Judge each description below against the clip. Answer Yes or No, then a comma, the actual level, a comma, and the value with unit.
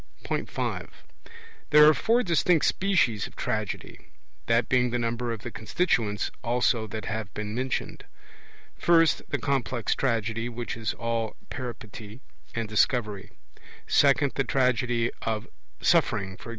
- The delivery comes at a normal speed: No, slow, 130 wpm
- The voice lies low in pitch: Yes, low, 120 Hz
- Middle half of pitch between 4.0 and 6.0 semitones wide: No, average, 3.3 semitones